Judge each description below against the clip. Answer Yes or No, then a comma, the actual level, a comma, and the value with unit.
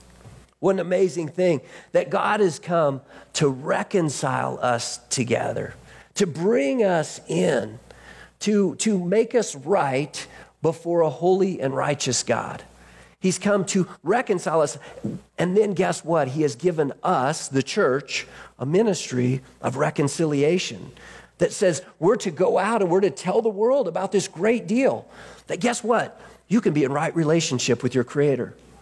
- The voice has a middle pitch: Yes, medium, 170 Hz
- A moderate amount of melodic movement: No, wide, 6.3 semitones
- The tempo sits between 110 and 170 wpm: Yes, average, 155 wpm